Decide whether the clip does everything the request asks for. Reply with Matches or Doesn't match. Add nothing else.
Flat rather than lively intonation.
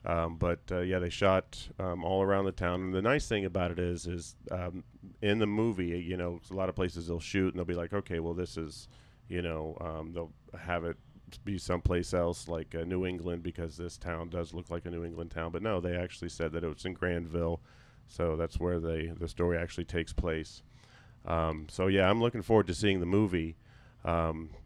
Matches